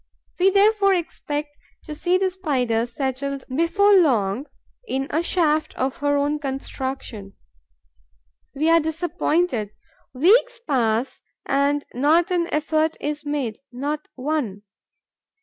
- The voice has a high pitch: Yes, very high, 295 Hz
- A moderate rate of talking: No, slow, 115 wpm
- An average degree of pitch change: Yes, average, 4.2 semitones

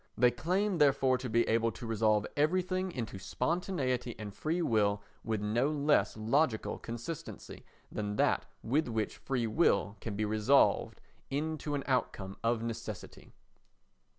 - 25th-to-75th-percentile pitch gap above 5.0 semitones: Yes, wide, 5.4 semitones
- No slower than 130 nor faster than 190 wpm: Yes, slow, 135 wpm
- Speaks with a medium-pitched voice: No, low, 120 Hz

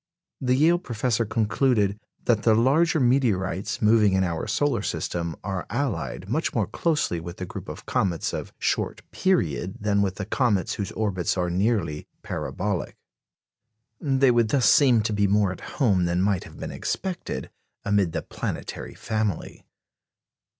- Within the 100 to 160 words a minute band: Yes, average, 155 wpm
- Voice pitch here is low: Yes, low, 105 Hz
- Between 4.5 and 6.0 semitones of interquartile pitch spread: Yes, average, 4.8 semitones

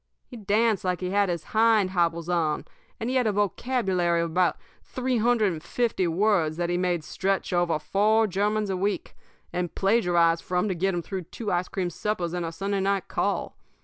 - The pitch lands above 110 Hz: Yes, high, 190 Hz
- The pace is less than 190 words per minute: No, average, 195 wpm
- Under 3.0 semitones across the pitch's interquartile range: No, average, 3.3 semitones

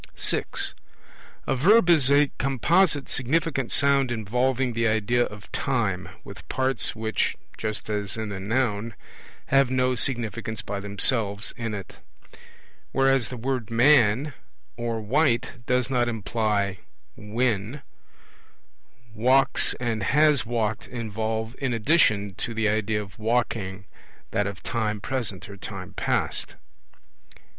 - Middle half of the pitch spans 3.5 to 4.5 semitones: Yes, average, 3.8 semitones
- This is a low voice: Yes, low, 115 Hz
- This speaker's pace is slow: Yes, slow, 125 wpm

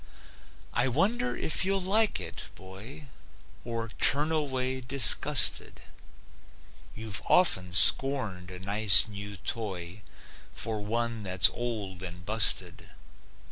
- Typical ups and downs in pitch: No, wide, 5.9 semitones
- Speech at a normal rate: No, slow, 105 wpm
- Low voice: Yes, low, 110 Hz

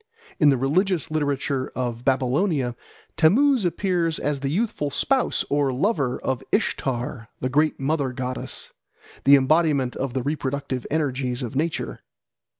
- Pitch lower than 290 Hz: Yes, medium, 140 Hz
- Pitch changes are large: No, average, 3.5 semitones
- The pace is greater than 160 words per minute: No, slow, 135 wpm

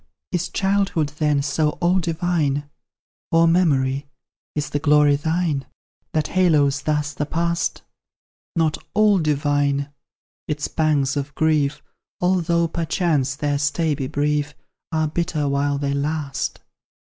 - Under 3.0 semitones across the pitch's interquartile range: Yes, narrow, 2.6 semitones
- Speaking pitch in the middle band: Yes, medium, 150 Hz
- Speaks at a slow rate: Yes, slow, 120 wpm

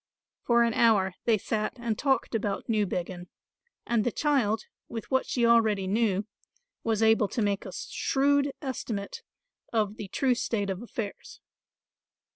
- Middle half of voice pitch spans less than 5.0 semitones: Yes, average, 2.7 semitones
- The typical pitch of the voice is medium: No, high, 225 Hz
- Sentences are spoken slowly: No, average, 145 wpm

